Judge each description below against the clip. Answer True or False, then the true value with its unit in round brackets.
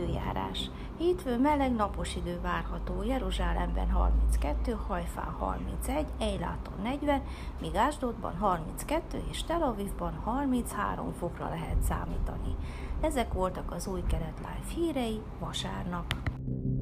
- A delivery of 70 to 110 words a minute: True (105 wpm)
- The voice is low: False (175 Hz)